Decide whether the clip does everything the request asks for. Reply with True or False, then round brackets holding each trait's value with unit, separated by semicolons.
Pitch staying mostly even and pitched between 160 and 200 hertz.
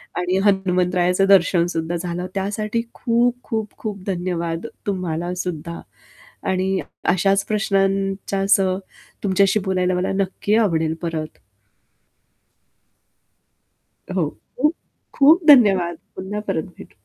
True (2.3 semitones; 190 Hz)